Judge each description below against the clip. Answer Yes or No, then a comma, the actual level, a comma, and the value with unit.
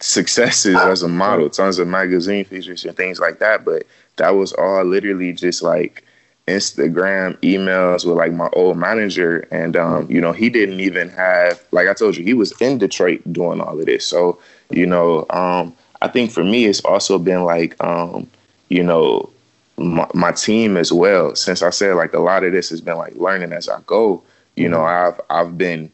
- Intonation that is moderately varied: No, narrow, 1.8 semitones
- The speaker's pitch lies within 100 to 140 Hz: No, very low, 90 Hz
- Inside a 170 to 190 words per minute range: No, average, 200 wpm